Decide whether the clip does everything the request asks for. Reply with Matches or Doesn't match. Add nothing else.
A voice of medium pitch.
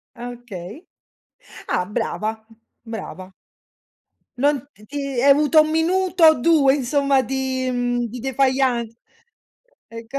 Doesn't match